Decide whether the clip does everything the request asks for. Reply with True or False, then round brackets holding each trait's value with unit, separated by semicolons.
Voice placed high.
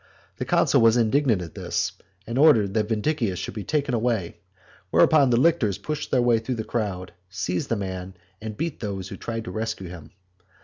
False (110 Hz)